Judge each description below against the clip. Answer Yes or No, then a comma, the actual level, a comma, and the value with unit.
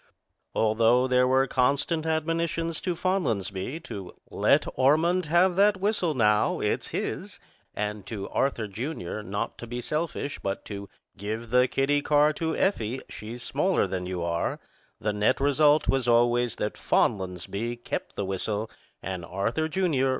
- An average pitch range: No, wide, 6.9 semitones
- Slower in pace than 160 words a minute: Yes, average, 150 wpm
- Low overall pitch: Yes, low, 125 Hz